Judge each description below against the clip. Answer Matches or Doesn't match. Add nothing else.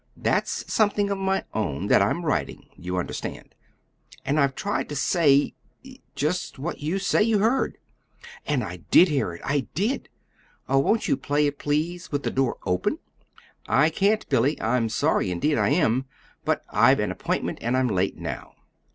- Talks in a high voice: Doesn't match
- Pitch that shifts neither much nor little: Doesn't match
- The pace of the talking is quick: Doesn't match